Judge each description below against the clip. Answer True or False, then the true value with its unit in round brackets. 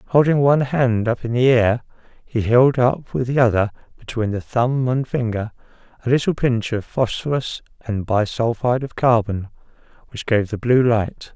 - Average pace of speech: True (175 wpm)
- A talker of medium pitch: False (120 Hz)